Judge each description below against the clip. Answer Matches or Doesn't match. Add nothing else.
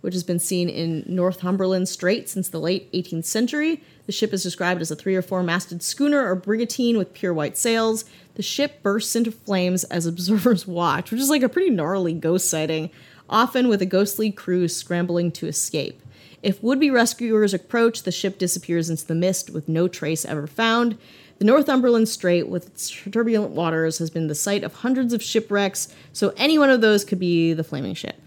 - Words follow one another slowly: Doesn't match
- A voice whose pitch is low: Doesn't match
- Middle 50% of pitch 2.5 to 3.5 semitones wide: Doesn't match